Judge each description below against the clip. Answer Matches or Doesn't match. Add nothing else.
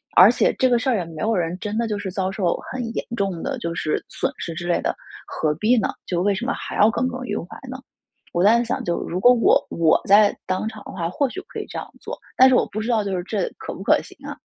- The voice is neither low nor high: Doesn't match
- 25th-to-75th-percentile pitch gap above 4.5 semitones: Matches